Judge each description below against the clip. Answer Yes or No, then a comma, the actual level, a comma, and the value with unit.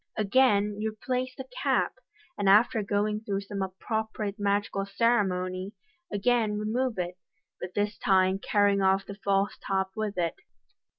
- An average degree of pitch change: No, narrow, 1.9 semitones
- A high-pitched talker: Yes, high, 205 Hz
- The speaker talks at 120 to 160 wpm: Yes, average, 145 wpm